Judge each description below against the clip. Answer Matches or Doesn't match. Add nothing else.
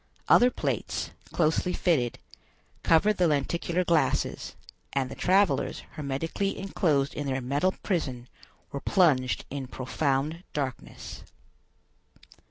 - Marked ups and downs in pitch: Doesn't match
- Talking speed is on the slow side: Matches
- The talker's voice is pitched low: Doesn't match